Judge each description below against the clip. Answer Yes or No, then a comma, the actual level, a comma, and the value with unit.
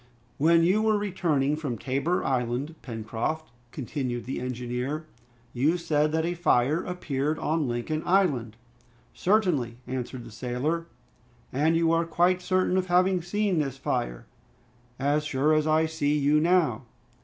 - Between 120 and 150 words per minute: Yes, average, 145 wpm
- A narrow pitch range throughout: No, average, 4.8 semitones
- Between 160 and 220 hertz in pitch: No, medium, 150 Hz